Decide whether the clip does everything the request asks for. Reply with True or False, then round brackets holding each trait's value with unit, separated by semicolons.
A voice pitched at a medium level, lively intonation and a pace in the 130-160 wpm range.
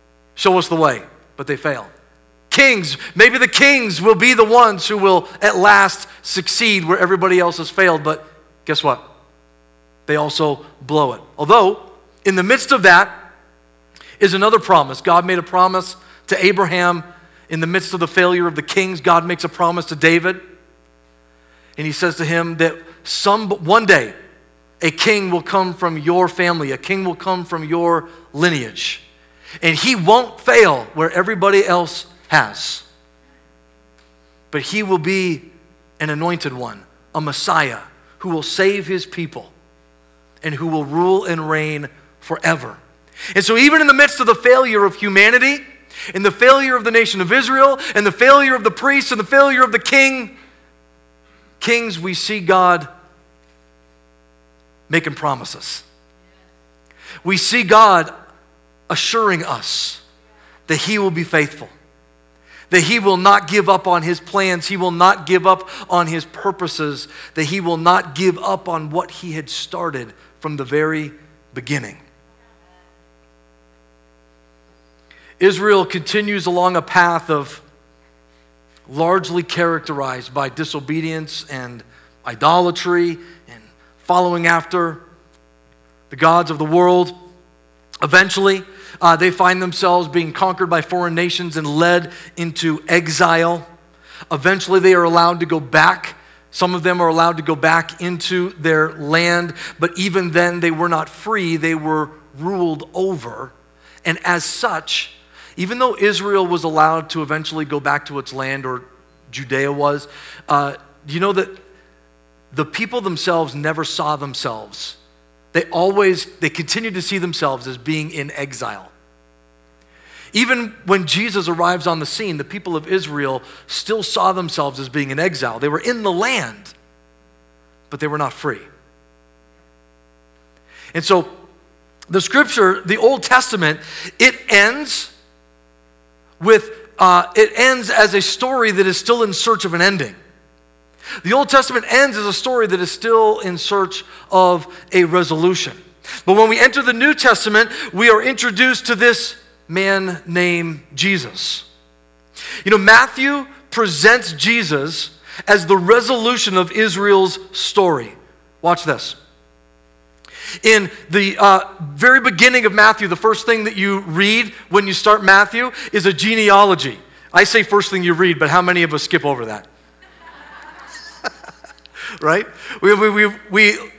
True (170 Hz; 6.3 semitones; 150 wpm)